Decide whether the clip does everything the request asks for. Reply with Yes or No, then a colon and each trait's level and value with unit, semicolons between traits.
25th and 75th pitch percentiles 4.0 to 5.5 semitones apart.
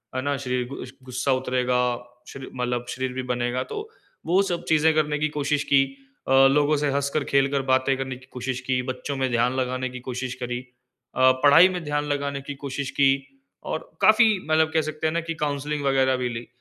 No: average, 2.7 semitones